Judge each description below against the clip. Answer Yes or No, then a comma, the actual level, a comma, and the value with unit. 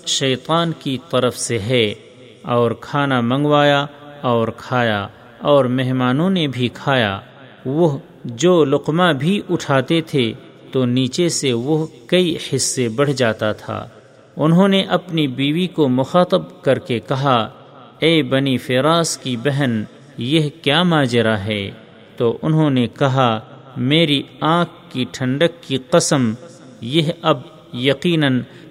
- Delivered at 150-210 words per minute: No, average, 130 wpm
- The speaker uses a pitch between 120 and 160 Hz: Yes, low, 135 Hz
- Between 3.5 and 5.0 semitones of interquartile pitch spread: Yes, average, 4.3 semitones